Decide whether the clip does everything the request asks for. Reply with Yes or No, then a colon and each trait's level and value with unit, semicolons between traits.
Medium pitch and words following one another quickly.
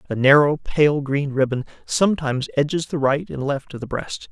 No: medium, 145 Hz; average, 195 wpm